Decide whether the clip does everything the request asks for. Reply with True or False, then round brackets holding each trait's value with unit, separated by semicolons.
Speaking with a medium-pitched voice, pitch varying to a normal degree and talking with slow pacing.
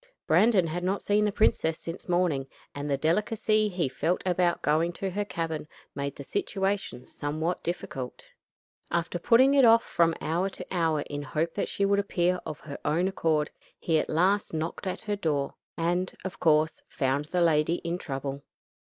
False (170 Hz; 3.9 semitones; 175 wpm)